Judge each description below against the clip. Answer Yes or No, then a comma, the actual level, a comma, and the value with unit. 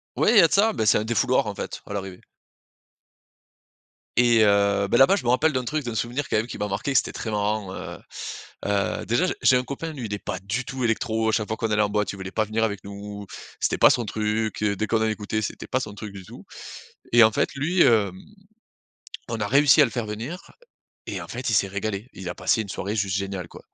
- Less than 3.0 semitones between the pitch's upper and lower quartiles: No, average, 3.3 semitones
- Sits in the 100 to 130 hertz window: Yes, low, 110 Hz